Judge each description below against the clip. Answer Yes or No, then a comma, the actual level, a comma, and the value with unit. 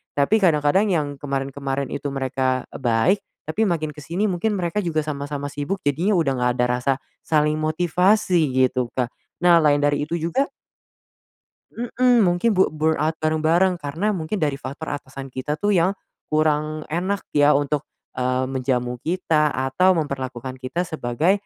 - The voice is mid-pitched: Yes, medium, 150 Hz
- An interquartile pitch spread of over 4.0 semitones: Yes, average, 4.4 semitones